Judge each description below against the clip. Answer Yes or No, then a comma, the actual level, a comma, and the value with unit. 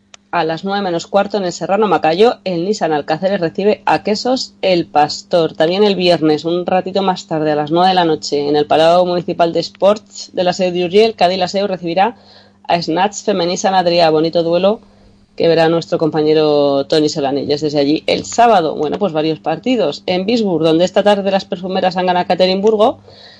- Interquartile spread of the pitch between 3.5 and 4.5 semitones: Yes, average, 3.8 semitones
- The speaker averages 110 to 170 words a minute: No, average, 185 wpm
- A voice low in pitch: No, medium, 175 Hz